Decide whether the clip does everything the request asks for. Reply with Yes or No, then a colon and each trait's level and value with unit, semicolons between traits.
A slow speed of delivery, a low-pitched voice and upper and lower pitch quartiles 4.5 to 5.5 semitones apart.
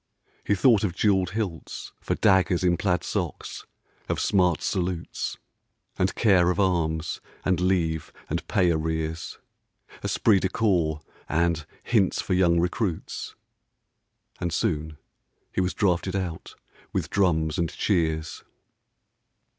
No: slow, 125 wpm; very low, 90 Hz; average, 2.8 semitones